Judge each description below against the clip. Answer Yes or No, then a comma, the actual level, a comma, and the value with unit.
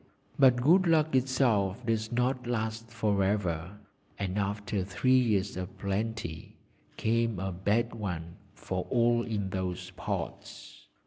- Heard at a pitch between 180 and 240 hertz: No, low, 110 Hz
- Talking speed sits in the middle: No, slow, 130 wpm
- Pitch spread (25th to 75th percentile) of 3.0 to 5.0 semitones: Yes, average, 3.7 semitones